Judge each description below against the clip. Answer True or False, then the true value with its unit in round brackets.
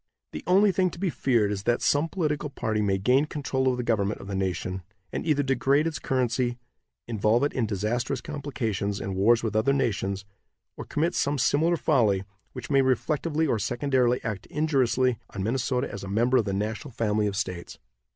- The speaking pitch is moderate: False (125 Hz)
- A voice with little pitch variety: False (5.3 semitones)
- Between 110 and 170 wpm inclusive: False (190 wpm)